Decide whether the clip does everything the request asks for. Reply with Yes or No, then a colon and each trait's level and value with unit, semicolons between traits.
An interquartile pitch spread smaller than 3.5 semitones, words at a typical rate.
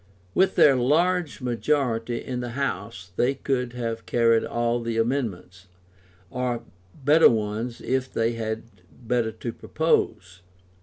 No: narrow, 2.5 semitones; slow, 125 wpm